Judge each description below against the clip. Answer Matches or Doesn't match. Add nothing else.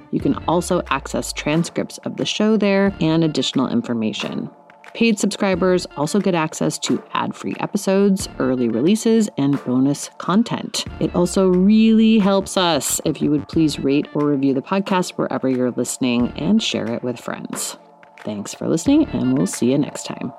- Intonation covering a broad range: Matches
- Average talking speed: Matches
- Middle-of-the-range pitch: Matches